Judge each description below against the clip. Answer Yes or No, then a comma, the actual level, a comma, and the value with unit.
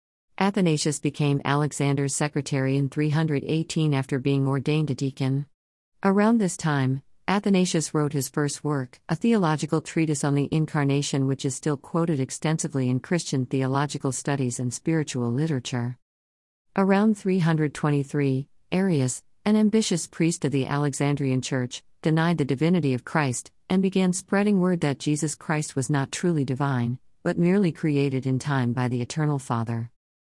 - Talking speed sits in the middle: No, fast, 145 wpm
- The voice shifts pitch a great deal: No, average, 3.3 semitones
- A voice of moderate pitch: Yes, medium, 145 Hz